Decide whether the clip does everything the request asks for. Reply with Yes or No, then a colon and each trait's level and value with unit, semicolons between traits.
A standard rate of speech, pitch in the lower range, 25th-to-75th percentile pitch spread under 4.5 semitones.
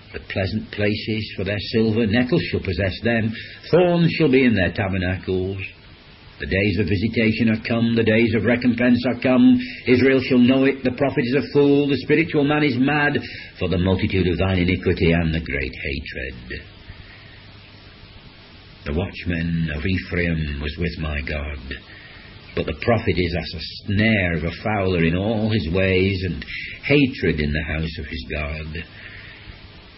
No: average, 165 wpm; low, 100 Hz; average, 5.2 semitones